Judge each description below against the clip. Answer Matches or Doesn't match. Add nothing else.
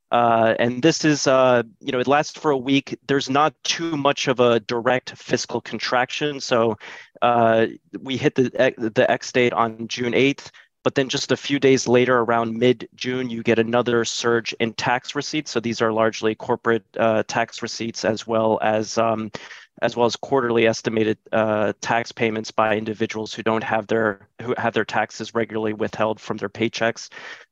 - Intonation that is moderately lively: Doesn't match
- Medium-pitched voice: Doesn't match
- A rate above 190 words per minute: Doesn't match